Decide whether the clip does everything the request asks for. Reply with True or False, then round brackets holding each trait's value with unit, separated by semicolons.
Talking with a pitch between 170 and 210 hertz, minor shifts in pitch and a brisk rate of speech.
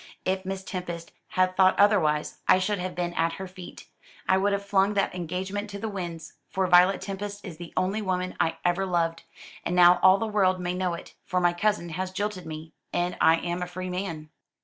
True (185 Hz; 1.8 semitones; 215 wpm)